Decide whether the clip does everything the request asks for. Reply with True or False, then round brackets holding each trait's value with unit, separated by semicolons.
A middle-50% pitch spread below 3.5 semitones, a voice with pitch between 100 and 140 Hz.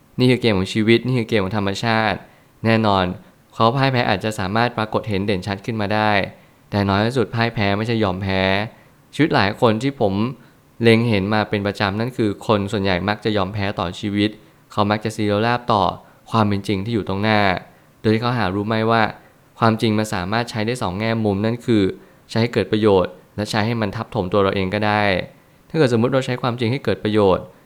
True (2.4 semitones; 110 Hz)